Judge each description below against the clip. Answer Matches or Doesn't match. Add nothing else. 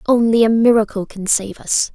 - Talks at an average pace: Matches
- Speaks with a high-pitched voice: Matches